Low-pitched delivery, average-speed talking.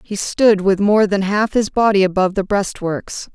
No: high, 200 Hz; average, 195 wpm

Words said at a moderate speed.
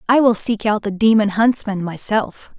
Yes: average, 185 wpm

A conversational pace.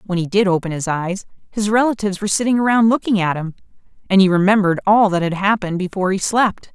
No: fast, 215 wpm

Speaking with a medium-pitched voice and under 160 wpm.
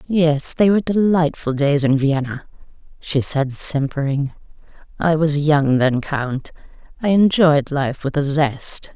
Yes: medium, 150 Hz; average, 140 wpm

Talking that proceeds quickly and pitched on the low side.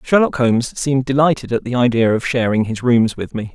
Yes: fast, 220 wpm; low, 125 Hz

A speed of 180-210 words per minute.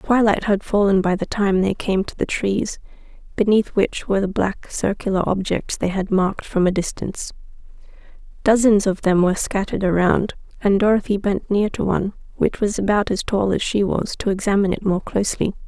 Yes: average, 190 wpm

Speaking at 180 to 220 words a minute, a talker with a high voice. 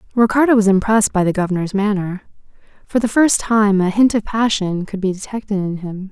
Yes: average, 195 wpm; high, 205 Hz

